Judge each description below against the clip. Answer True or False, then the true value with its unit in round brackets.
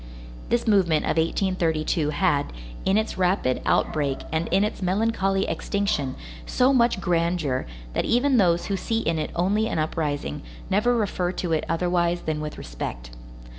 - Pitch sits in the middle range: True (175 Hz)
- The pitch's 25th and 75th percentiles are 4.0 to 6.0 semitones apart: True (4.4 semitones)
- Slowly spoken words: False (155 wpm)